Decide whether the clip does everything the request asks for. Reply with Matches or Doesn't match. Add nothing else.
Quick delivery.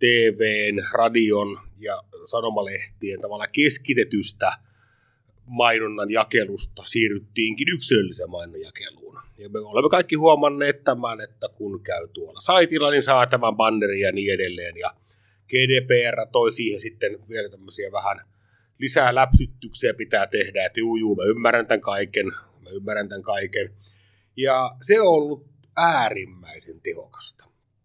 Doesn't match